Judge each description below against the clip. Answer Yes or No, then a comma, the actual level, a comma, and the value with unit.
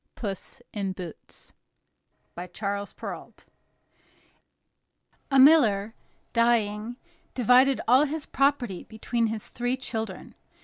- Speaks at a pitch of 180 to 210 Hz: No, high, 225 Hz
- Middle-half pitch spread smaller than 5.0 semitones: Yes, average, 4.1 semitones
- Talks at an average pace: No, slow, 95 wpm